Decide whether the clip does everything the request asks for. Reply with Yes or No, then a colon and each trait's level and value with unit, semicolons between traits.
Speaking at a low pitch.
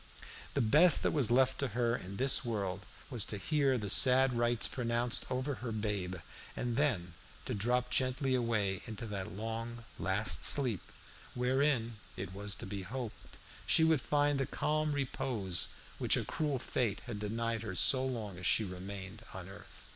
Yes: low, 115 Hz